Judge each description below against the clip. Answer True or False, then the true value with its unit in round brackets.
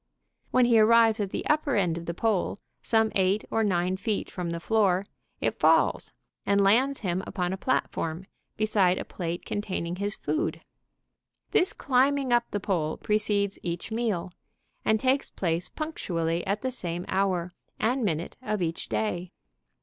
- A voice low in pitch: False (200 Hz)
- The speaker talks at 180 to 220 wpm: False (160 wpm)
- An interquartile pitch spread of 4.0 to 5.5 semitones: True (4.3 semitones)